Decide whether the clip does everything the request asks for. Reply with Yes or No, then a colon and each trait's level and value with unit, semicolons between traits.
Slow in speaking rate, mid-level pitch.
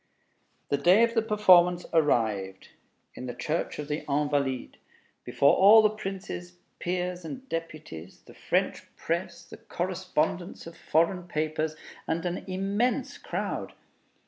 Yes: slow, 130 wpm; medium, 170 Hz